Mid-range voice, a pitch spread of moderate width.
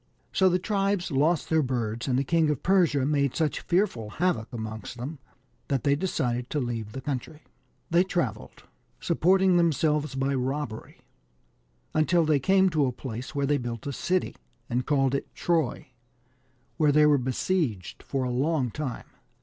Yes: medium, 145 Hz; average, 4.9 semitones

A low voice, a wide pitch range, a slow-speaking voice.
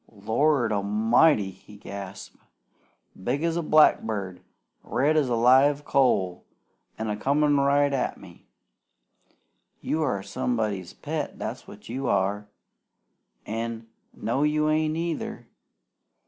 Yes: low, 120 Hz; wide, 5.9 semitones; slow, 120 wpm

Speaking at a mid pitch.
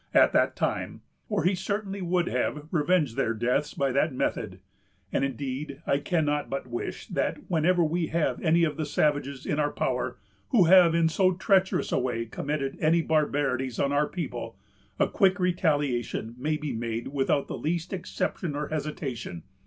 Yes: medium, 150 Hz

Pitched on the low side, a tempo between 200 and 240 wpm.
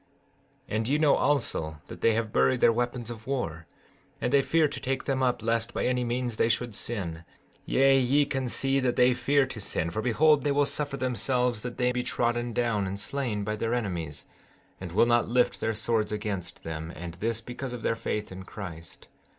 Yes: low, 120 Hz; fast, 205 wpm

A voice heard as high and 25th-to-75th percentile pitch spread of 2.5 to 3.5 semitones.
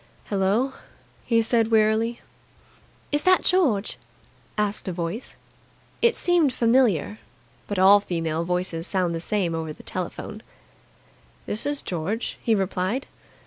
No: high, 210 Hz; average, 4.6 semitones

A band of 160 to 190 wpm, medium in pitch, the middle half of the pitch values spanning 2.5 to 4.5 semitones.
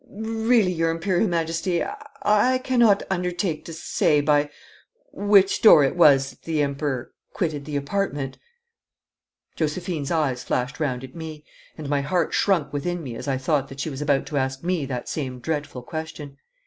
Yes: average, 165 wpm; medium, 155 Hz; average, 4.2 semitones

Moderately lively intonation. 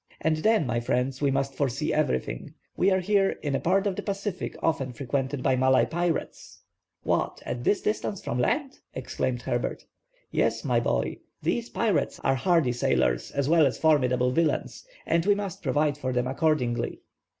No: wide, 6.1 semitones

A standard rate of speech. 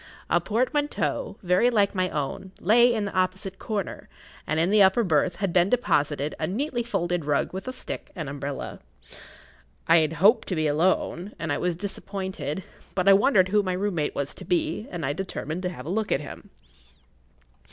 Yes: average, 195 wpm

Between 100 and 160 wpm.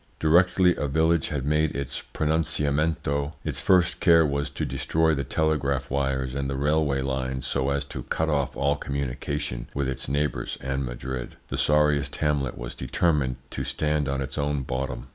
No: average, 170 wpm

